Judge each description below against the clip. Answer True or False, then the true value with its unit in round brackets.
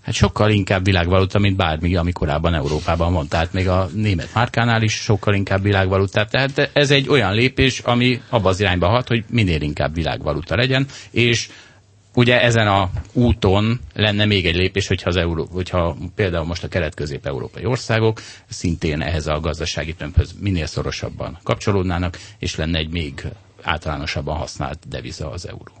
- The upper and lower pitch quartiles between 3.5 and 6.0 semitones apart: True (4.7 semitones)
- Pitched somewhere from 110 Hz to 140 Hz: False (95 Hz)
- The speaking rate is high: True (160 wpm)